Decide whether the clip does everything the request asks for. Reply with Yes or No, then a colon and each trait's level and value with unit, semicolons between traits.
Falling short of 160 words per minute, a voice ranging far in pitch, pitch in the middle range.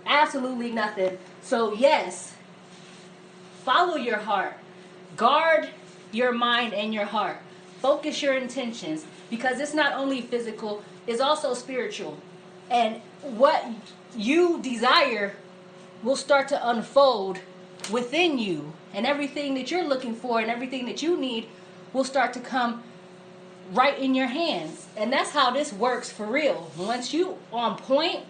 No: slow, 135 wpm; wide, 6.5 semitones; high, 235 Hz